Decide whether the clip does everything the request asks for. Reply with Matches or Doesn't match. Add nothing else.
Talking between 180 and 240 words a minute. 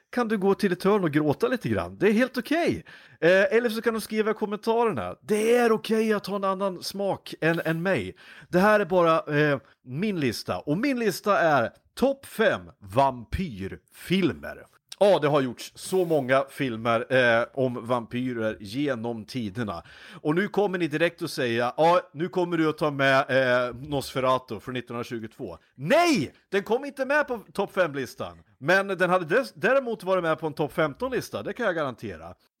Matches